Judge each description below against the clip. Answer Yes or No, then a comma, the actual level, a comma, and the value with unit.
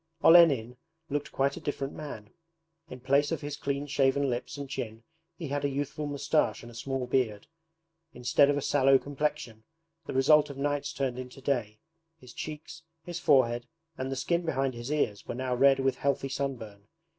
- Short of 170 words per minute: No, average, 180 wpm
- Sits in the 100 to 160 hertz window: Yes, low, 135 Hz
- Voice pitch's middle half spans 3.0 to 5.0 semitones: No, narrow, 2.5 semitones